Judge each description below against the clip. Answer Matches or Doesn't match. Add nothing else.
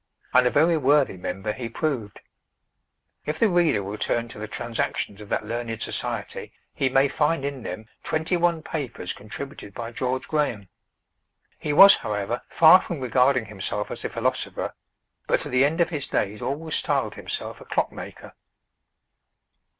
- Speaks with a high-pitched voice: Doesn't match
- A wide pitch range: Matches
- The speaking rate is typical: Matches